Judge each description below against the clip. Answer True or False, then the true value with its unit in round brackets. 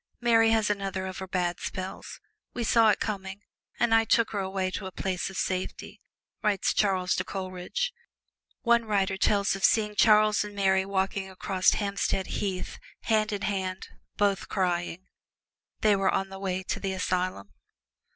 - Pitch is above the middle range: True (195 Hz)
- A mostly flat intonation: True (2.0 semitones)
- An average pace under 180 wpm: True (165 wpm)